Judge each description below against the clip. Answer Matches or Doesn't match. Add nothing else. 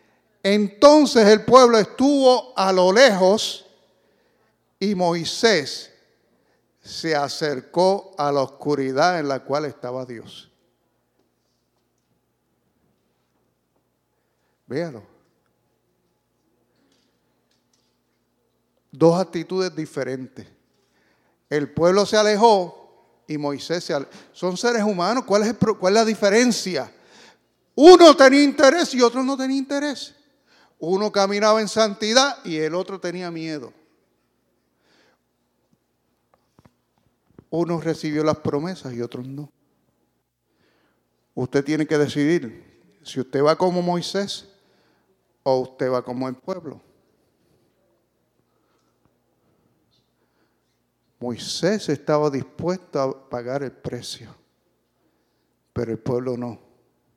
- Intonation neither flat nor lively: Doesn't match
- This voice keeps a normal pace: Doesn't match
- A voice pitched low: Doesn't match